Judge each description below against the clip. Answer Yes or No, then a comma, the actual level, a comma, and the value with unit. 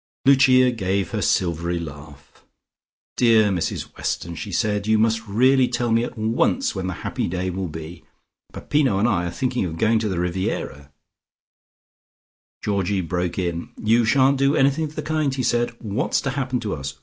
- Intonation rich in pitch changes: Yes, wide, 6.0 semitones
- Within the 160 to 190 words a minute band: Yes, average, 180 wpm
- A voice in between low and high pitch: No, low, 105 Hz